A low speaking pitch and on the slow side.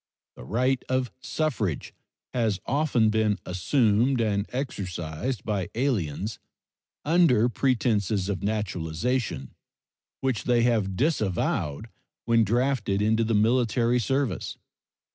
Yes: low, 110 Hz; slow, 105 wpm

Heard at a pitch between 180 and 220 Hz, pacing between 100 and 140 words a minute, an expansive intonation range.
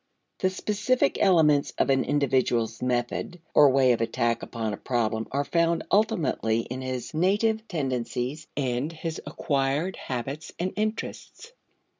No: medium, 140 Hz; slow, 135 wpm; wide, 6.0 semitones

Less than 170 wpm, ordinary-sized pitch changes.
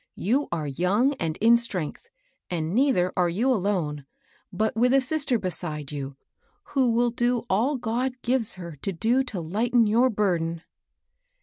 No: average, 160 wpm; wide, 6.3 semitones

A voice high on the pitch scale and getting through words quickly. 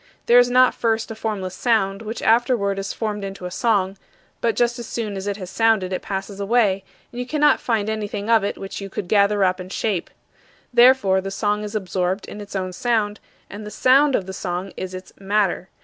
Yes: high, 205 Hz; fast, 215 wpm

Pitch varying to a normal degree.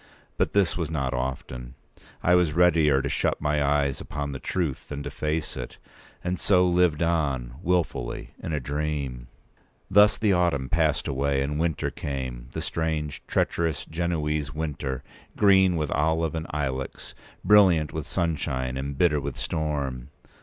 Yes: average, 3.6 semitones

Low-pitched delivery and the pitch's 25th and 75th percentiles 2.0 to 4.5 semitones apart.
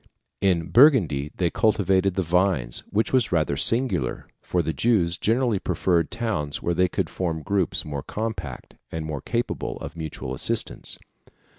No: very low, 90 Hz; wide, 5.4 semitones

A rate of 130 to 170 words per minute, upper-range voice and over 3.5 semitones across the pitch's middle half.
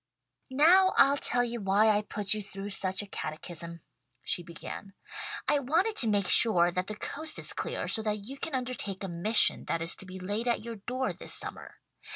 No: average, 200 wpm; high, 210 Hz; average, 4.9 semitones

